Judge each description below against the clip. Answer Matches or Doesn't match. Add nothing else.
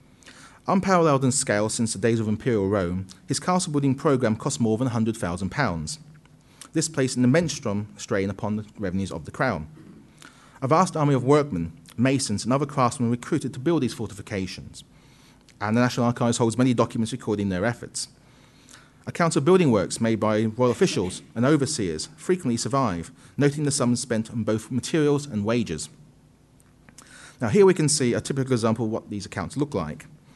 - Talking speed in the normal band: Matches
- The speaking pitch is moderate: Doesn't match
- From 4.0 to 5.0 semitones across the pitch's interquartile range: Matches